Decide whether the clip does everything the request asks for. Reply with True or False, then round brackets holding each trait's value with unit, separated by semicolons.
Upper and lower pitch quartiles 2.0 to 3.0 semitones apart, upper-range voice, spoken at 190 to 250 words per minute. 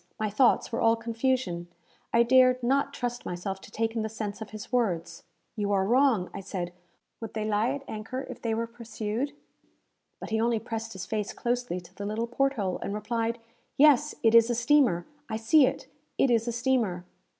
True (2.7 semitones; 225 Hz; 200 wpm)